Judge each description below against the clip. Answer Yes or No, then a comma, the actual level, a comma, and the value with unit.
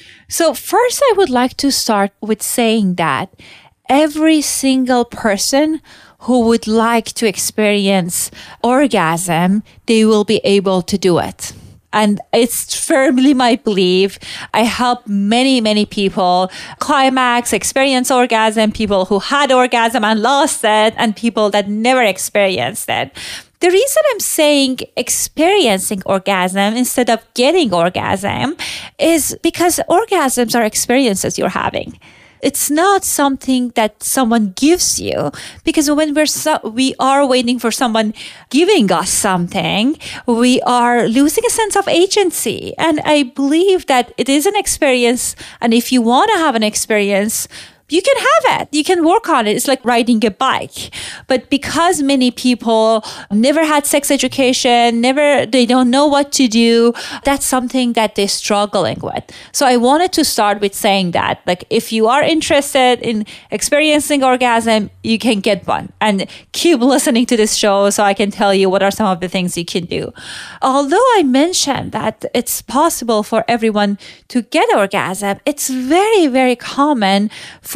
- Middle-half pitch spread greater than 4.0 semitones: Yes, average, 5.1 semitones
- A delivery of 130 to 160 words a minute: Yes, average, 155 wpm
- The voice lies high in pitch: Yes, high, 245 Hz